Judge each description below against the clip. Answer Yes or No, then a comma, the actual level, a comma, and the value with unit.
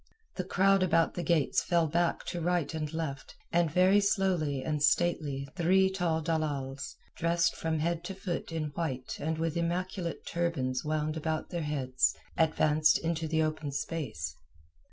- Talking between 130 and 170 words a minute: Yes, average, 155 wpm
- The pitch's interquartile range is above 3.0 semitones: No, narrow, 2.4 semitones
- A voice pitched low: No, medium, 160 Hz